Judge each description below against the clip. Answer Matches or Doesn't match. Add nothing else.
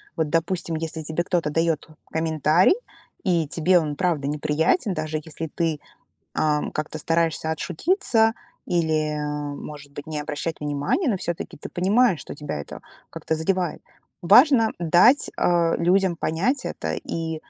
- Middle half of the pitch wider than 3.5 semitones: Doesn't match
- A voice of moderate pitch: Matches